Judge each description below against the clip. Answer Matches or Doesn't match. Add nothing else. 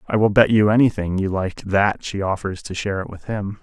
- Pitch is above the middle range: Doesn't match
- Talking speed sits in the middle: Doesn't match